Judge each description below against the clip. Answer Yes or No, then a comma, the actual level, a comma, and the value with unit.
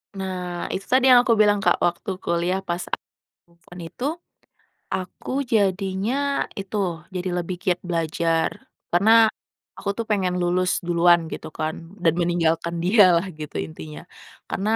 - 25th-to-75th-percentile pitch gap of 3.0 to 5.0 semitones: No, narrow, 2.4 semitones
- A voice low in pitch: No, medium, 180 Hz